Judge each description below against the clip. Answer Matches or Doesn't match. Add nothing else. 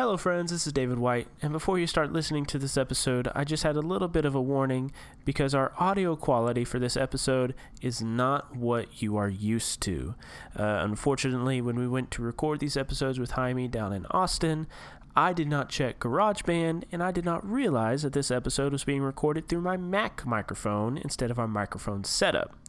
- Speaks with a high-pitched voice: Doesn't match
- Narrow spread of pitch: Doesn't match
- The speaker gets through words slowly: Doesn't match